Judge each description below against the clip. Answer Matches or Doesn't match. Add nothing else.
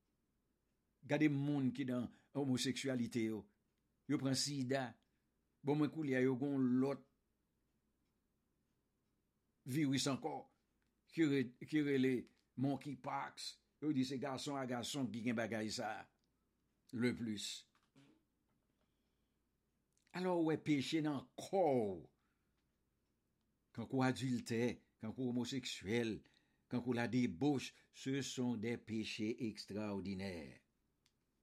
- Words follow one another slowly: Matches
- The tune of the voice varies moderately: Matches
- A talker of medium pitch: Doesn't match